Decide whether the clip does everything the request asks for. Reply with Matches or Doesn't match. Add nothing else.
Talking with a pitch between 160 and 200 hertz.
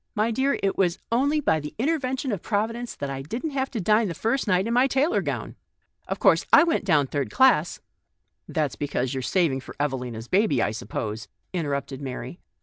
Matches